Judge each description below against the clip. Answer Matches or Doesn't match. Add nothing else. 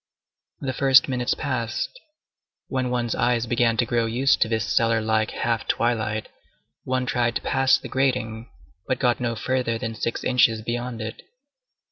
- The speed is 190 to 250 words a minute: Doesn't match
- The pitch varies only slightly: Matches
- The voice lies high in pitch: Doesn't match